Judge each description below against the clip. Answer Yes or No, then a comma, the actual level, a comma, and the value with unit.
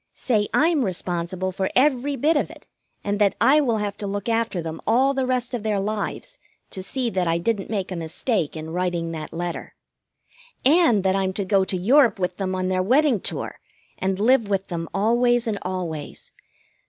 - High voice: Yes, high, 200 Hz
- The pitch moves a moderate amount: Yes, average, 4.8 semitones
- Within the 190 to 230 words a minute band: Yes, average, 195 wpm